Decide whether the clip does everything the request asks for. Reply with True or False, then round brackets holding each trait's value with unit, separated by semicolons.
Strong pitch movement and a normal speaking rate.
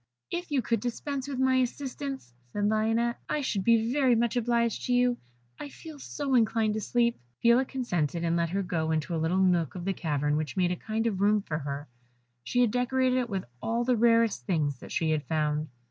False (6.4 semitones; 215 wpm)